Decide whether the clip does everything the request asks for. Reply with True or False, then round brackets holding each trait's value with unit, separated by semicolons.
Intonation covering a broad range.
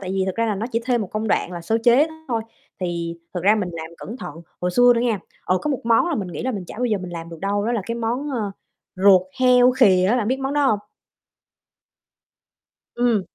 False (4.8 semitones)